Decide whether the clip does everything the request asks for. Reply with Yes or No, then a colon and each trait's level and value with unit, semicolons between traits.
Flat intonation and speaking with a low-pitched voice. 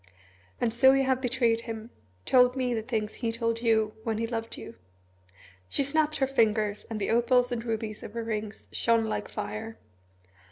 No: narrow, 2.0 semitones; high, 230 Hz